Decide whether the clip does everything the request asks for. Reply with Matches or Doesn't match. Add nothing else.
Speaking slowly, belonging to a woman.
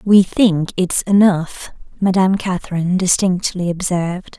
Matches